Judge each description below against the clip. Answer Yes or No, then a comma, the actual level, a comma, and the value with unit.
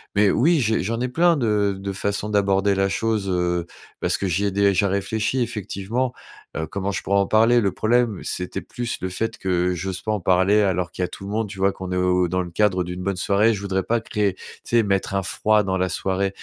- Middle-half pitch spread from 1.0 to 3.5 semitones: Yes, narrow, 2.6 semitones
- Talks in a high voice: No, low, 100 Hz